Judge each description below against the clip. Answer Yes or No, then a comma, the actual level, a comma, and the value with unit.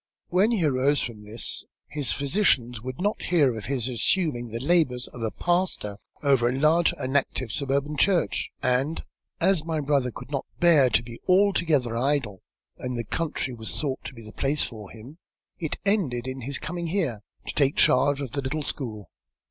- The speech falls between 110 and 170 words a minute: No, average, 185 wpm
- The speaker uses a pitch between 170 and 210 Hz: No, low, 135 Hz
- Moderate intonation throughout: Yes, average, 4.8 semitones